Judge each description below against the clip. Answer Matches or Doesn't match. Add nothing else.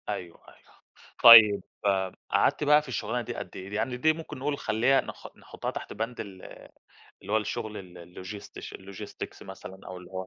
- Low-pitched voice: Matches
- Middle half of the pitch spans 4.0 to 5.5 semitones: Matches